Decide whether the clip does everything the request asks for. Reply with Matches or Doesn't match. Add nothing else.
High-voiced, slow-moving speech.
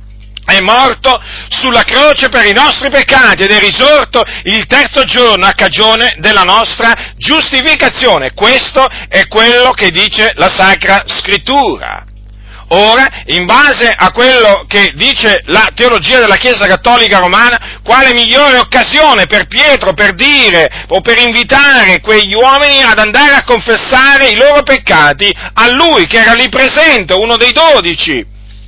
Doesn't match